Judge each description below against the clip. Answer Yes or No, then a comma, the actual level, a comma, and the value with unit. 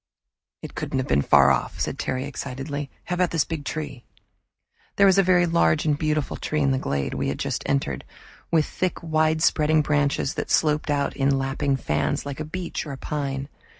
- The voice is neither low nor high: Yes, medium, 145 Hz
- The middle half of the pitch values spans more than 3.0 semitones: No, narrow, 2.6 semitones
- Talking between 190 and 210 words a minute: Yes, average, 195 wpm